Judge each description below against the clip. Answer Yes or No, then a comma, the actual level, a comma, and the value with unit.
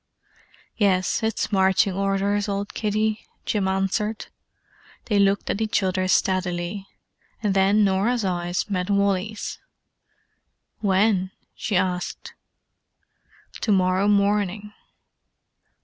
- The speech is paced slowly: Yes, slow, 100 wpm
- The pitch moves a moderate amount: No, narrow, 1.7 semitones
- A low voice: No, high, 200 Hz